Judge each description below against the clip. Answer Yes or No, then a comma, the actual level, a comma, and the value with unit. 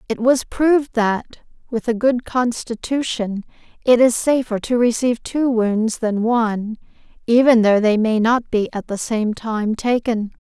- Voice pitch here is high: Yes, high, 230 Hz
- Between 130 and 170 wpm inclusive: Yes, average, 160 wpm